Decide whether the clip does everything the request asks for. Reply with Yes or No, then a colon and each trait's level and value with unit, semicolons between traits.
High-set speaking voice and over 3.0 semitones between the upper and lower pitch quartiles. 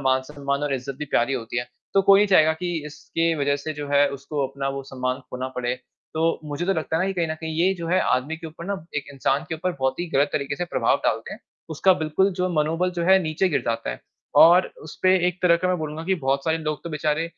No: medium, 155 Hz; average, 3.5 semitones